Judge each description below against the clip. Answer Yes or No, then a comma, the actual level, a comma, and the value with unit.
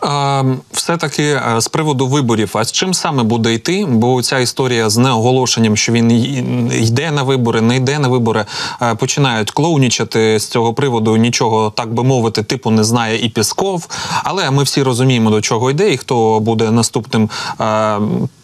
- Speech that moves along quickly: Yes, fast, 165 wpm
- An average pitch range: Yes, average, 3.2 semitones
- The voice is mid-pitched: No, low, 120 Hz